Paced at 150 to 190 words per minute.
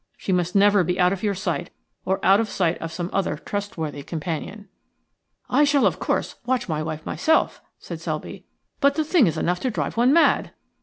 No: fast, 205 wpm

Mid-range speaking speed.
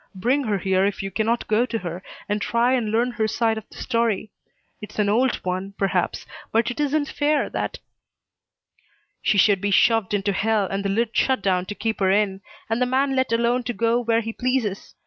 No: fast, 215 wpm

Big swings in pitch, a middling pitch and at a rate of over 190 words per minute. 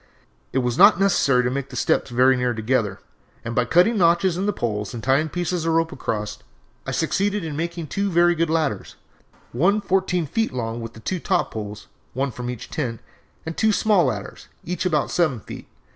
Yes: wide, 6.5 semitones; medium, 155 Hz; average, 200 wpm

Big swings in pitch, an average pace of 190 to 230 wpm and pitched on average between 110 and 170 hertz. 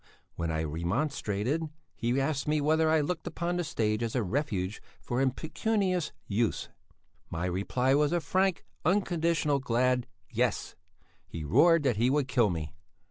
No: wide, 6.9 semitones; average, 150 wpm; low, 135 Hz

